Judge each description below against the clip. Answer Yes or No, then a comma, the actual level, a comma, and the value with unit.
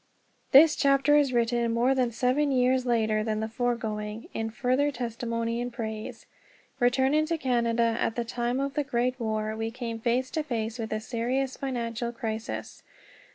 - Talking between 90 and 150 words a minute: No, average, 165 wpm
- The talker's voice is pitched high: Yes, high, 240 Hz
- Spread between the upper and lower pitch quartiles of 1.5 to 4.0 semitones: Yes, narrow, 2.4 semitones